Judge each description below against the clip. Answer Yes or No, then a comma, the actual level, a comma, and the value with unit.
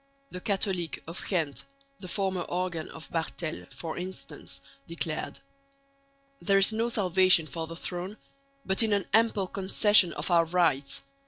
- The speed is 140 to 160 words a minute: Yes, average, 145 wpm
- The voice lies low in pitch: No, medium, 180 Hz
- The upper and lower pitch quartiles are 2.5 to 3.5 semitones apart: Yes, average, 2.9 semitones